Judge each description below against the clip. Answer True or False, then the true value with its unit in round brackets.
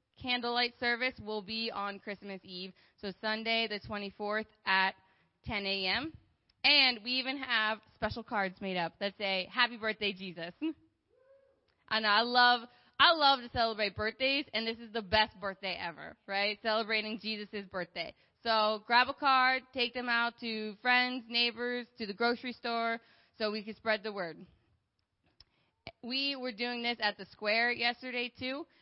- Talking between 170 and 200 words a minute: False (160 wpm)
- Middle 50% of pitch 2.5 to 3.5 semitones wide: True (2.9 semitones)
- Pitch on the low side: False (225 Hz)